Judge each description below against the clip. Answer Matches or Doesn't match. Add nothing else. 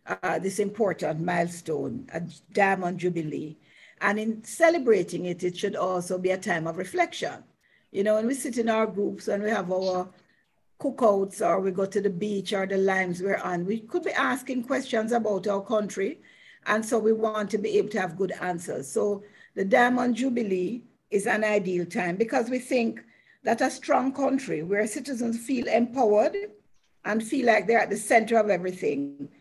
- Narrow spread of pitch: Doesn't match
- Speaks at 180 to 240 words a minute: Matches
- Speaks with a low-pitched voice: Doesn't match